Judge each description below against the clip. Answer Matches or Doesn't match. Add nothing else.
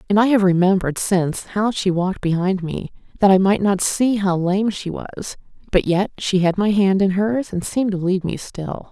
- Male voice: Doesn't match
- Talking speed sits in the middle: Doesn't match